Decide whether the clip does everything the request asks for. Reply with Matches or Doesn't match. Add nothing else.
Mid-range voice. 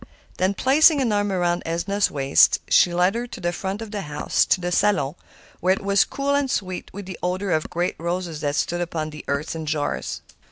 Matches